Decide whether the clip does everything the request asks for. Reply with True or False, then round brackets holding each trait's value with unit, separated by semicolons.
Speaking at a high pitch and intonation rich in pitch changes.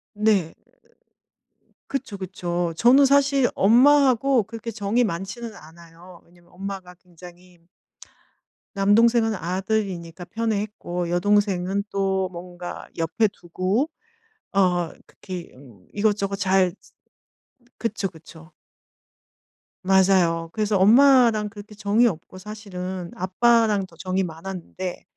False (195 Hz; 3.5 semitones)